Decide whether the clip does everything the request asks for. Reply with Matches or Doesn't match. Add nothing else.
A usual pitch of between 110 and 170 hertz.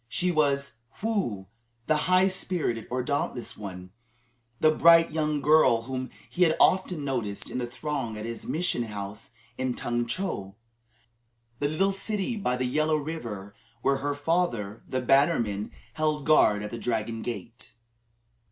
Matches